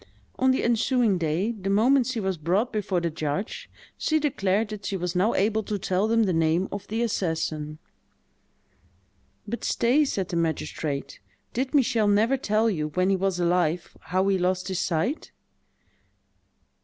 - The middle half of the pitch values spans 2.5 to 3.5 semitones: No, average, 4.4 semitones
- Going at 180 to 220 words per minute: No, average, 165 wpm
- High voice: Yes, high, 195 Hz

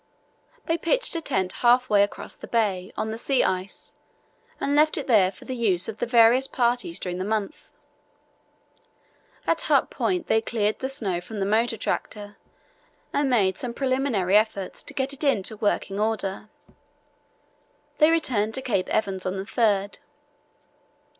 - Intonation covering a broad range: No, average, 4.7 semitones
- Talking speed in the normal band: Yes, average, 160 wpm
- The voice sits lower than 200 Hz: No, high, 220 Hz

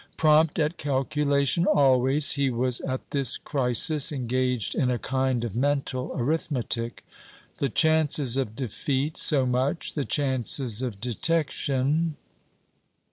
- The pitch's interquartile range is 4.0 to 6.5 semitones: No, average, 2.9 semitones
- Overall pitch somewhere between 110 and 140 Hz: Yes, low, 135 Hz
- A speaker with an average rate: No, slow, 120 wpm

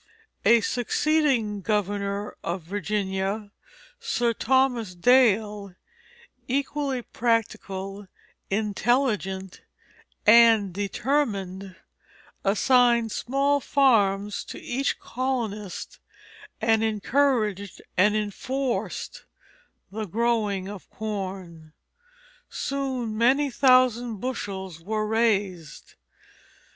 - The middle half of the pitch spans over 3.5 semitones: Yes, average, 3.9 semitones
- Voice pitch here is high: Yes, high, 215 Hz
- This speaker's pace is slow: Yes, slow, 75 wpm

